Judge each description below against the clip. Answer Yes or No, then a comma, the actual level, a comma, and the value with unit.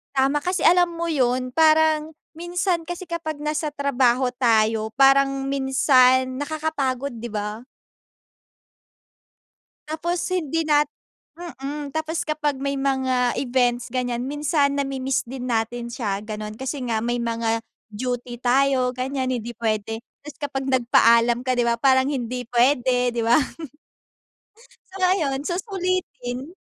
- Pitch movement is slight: No, average, 3.7 semitones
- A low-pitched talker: No, very high, 265 Hz